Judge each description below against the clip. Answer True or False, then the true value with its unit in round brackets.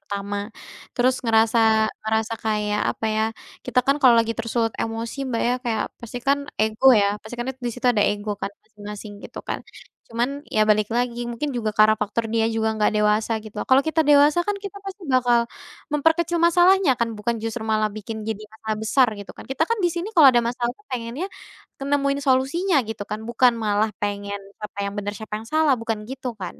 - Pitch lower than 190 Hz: False (230 Hz)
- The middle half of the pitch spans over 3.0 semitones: True (3.7 semitones)